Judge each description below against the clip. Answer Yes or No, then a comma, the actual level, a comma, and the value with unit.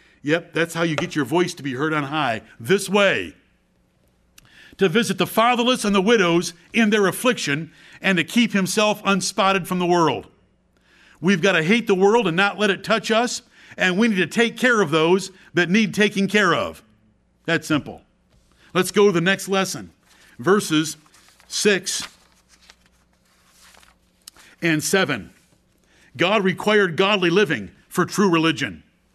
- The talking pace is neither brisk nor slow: Yes, average, 155 wpm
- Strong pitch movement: No, average, 4.4 semitones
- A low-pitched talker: No, medium, 185 Hz